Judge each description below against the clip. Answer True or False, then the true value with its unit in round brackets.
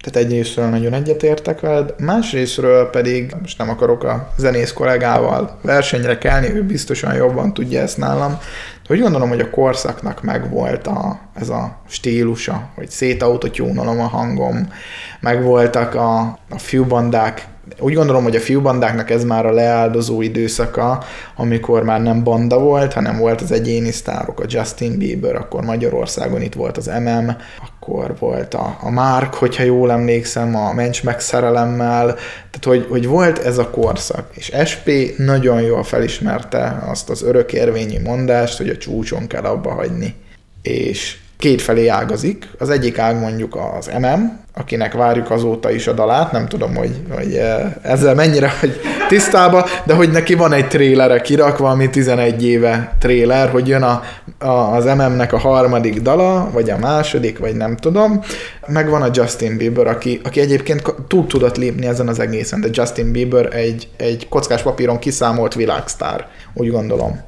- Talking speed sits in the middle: False (160 wpm)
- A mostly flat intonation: False (3.0 semitones)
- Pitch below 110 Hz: False (120 Hz)